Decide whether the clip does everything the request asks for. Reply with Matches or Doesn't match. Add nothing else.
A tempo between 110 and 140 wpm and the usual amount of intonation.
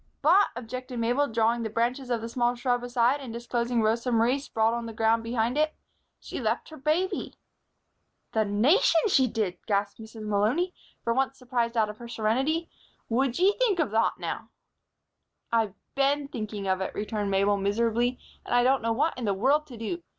Doesn't match